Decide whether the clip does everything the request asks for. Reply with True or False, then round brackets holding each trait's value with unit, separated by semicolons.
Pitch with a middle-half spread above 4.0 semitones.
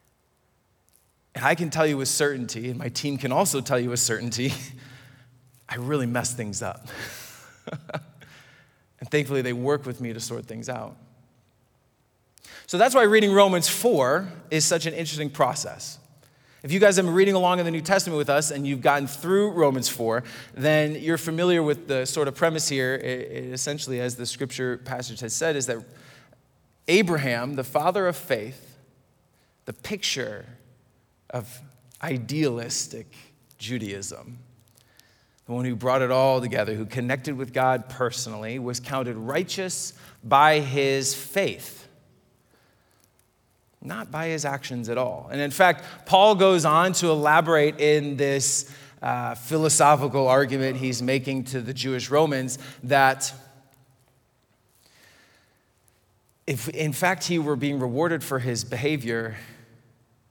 False (3.4 semitones)